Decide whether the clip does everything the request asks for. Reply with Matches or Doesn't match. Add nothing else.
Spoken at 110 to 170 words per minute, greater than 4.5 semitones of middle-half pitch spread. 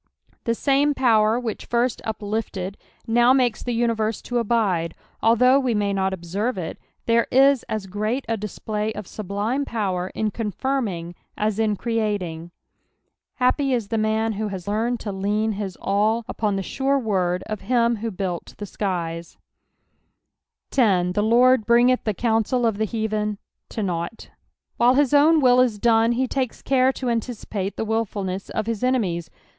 Doesn't match